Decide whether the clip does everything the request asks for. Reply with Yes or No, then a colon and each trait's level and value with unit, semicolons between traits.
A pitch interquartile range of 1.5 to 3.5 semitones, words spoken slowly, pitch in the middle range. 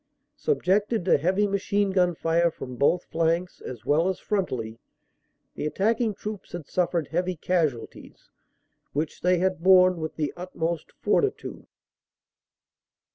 Yes: average, 2.9 semitones; slow, 130 wpm; medium, 180 Hz